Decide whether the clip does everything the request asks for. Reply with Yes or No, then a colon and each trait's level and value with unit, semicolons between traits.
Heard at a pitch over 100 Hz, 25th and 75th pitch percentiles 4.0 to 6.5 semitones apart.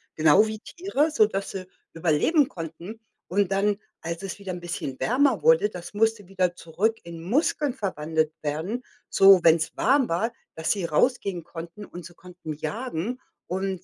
Yes: high, 190 Hz; average, 4.9 semitones